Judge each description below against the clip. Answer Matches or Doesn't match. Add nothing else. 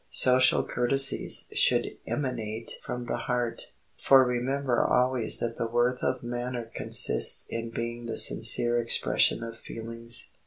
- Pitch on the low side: Matches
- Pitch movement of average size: Doesn't match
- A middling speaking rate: Doesn't match